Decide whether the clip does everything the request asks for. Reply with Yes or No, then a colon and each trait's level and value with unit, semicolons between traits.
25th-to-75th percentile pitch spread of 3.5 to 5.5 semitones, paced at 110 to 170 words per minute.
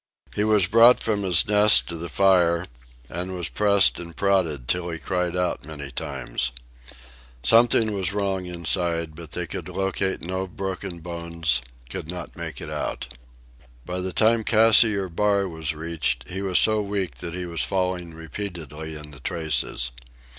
No: average, 3.1 semitones; average, 160 wpm